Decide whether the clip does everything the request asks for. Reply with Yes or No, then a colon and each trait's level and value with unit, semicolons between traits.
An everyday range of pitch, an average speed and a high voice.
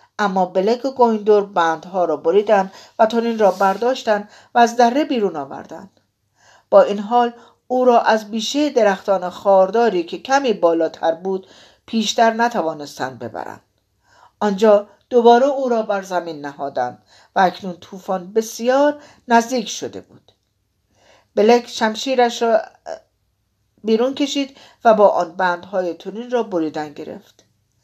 Yes: average, 4.7 semitones; average, 125 wpm; high, 215 Hz